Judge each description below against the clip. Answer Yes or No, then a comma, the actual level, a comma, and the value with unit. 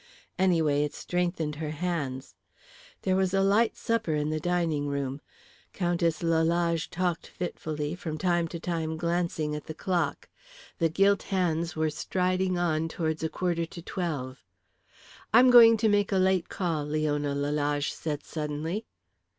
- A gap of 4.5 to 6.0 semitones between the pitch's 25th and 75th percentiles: No, average, 3.0 semitones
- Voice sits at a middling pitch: Yes, medium, 165 Hz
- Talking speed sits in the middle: Yes, average, 150 wpm